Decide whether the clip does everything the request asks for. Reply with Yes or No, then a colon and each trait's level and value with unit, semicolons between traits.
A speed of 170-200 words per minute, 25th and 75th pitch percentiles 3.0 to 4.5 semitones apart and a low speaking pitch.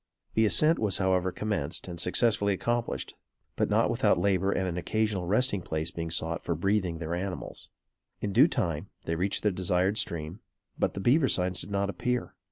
Yes: average, 180 wpm; average, 3.6 semitones; very low, 95 Hz